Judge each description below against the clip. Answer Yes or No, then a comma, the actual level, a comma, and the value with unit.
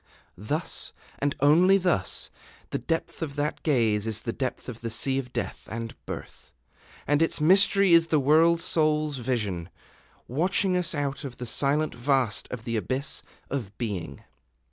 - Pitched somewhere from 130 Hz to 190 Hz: Yes, medium, 140 Hz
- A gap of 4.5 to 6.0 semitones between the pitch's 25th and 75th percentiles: Yes, wide, 5.5 semitones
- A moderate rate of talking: Yes, average, 160 wpm